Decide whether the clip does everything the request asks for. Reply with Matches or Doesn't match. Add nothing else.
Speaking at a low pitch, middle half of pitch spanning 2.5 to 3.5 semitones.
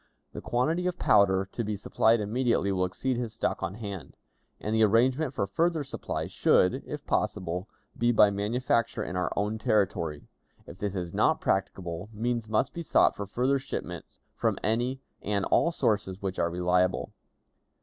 Doesn't match